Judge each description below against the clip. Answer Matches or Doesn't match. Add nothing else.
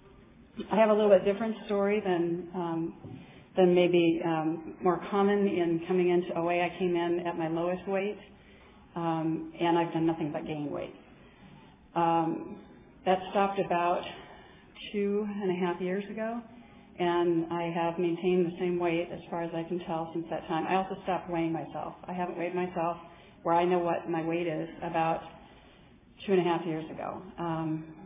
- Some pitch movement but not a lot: Doesn't match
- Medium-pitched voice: Matches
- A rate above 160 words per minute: Matches